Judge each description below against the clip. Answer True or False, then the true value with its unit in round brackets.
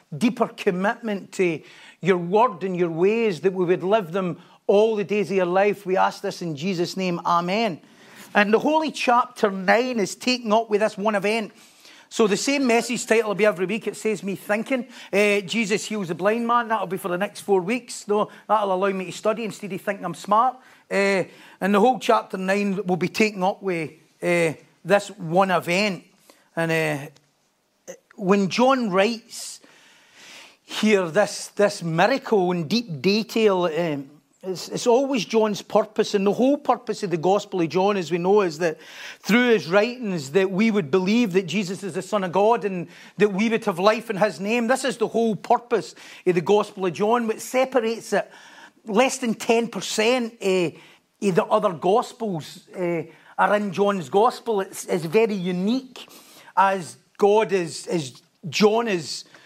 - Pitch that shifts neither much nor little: True (3.1 semitones)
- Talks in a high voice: True (205 Hz)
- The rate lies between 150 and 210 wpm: True (180 wpm)